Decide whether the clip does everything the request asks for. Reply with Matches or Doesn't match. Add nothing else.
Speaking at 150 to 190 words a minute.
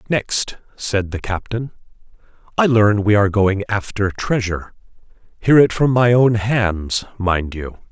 Doesn't match